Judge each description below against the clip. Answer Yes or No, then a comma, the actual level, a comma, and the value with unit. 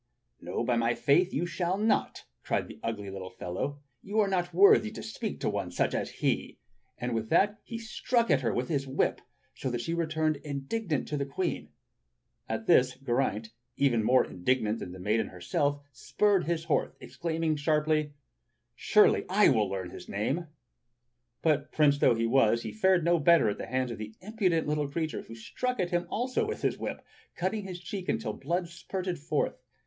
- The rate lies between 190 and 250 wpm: Yes, average, 195 wpm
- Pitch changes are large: Yes, wide, 6.7 semitones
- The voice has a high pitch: No, medium, 150 Hz